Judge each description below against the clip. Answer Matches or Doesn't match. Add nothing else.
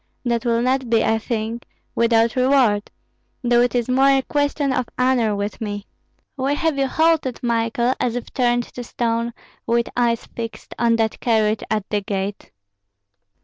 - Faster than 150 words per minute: Matches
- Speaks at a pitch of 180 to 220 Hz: Doesn't match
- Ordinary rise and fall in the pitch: Doesn't match